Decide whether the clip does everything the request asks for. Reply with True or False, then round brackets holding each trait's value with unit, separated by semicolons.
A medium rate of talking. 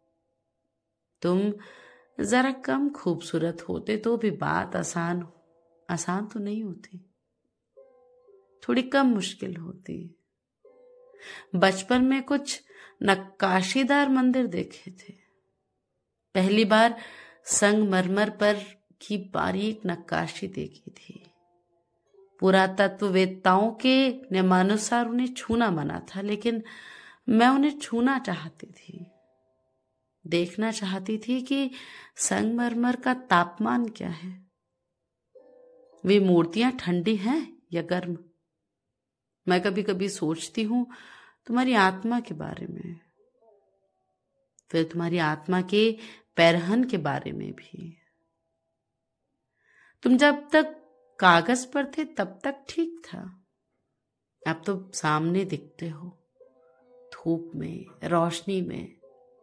False (100 wpm)